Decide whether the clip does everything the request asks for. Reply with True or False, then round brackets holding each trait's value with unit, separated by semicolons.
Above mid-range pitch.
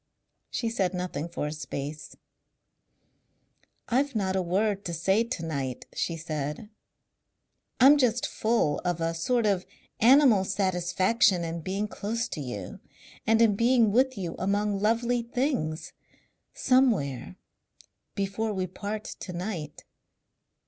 True (195 Hz)